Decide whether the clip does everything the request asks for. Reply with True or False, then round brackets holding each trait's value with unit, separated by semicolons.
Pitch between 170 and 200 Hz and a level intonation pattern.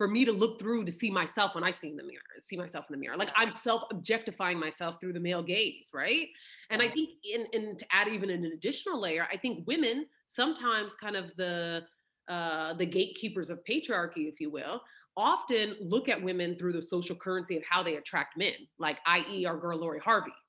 False (185 Hz; 4.9 semitones)